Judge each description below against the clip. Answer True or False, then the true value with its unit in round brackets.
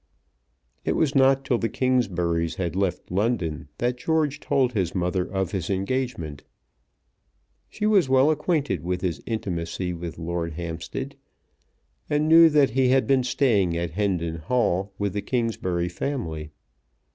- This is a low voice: True (100 Hz)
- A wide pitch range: True (7.3 semitones)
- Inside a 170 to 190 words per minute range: False (145 wpm)